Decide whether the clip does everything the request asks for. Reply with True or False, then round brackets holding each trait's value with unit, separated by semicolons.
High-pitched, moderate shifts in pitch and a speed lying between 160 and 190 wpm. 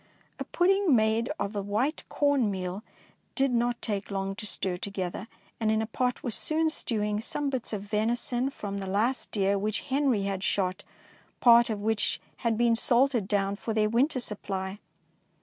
True (220 Hz; 3.5 semitones; 180 wpm)